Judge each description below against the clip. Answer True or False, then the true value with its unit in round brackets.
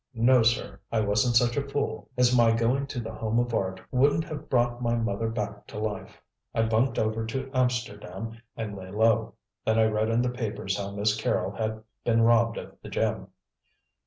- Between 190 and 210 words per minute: True (195 wpm)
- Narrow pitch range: True (2.2 semitones)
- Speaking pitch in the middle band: False (115 Hz)